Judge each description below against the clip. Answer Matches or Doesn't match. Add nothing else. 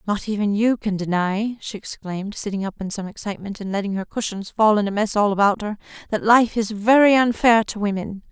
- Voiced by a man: Doesn't match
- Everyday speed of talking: Doesn't match